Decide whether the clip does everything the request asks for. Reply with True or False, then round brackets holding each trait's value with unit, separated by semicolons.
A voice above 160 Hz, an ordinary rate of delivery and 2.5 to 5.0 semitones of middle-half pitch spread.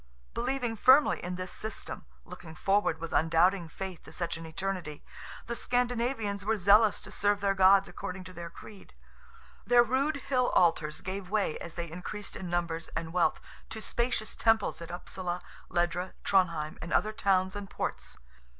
True (190 Hz; 160 wpm; 4.0 semitones)